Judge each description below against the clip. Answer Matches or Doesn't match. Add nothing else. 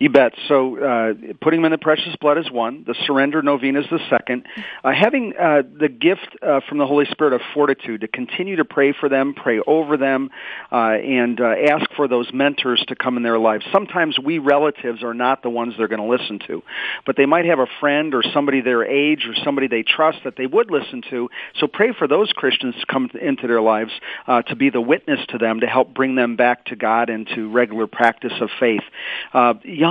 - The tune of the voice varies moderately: Matches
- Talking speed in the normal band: Doesn't match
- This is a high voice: Doesn't match